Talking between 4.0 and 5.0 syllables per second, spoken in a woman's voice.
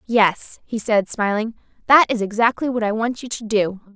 Yes: 4.8 syllables/s; female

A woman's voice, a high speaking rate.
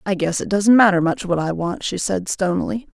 Yes: female; fast, 245 wpm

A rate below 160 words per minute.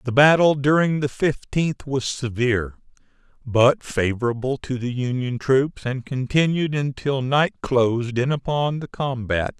Yes: average, 140 wpm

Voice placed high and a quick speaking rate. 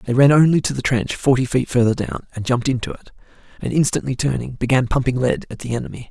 No: low, 130 Hz; fast, 225 wpm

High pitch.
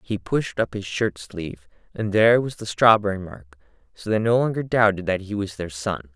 No: low, 100 Hz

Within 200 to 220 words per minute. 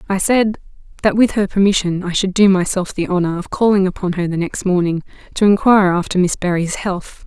Yes: fast, 205 wpm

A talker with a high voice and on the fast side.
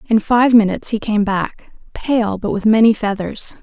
No: high, 215 Hz; average, 180 wpm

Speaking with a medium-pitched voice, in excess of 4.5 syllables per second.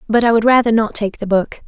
No: high, 220 Hz; 6.0 syllables/s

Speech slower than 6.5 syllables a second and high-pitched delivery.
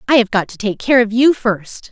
Yes: 5.2 syllables/s; high, 225 Hz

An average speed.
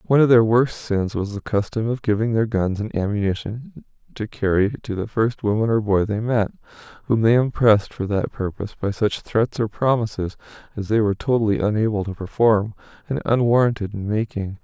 Yes: average, 190 wpm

